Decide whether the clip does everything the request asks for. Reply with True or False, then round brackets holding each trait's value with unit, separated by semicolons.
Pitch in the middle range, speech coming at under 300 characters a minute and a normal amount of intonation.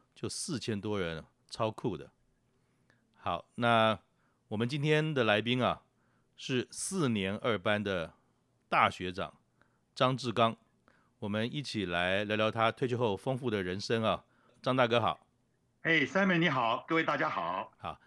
False (115 Hz; 210 characters per minute; 3.5 semitones)